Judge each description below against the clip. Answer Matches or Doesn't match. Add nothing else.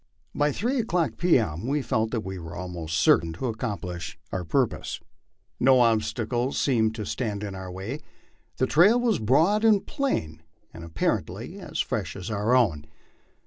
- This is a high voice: Doesn't match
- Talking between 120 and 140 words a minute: Doesn't match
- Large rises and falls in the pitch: Matches